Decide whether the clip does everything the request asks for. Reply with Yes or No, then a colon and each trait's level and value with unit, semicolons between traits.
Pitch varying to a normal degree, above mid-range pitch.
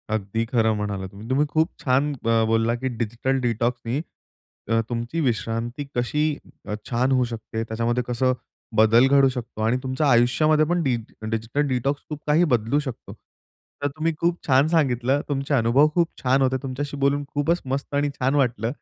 No: average, 3.7 semitones; low, 130 Hz